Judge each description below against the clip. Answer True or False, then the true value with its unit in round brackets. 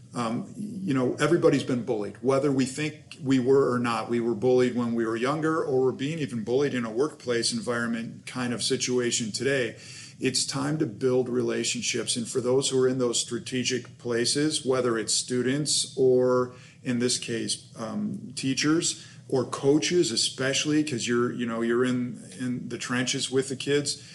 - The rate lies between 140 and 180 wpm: True (175 wpm)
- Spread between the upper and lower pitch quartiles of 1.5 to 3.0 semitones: True (2.7 semitones)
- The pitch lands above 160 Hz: False (130 Hz)